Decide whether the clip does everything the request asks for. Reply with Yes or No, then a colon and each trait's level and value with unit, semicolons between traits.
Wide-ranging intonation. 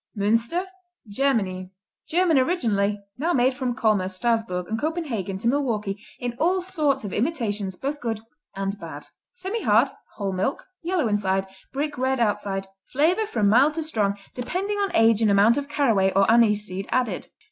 Yes: wide, 6.3 semitones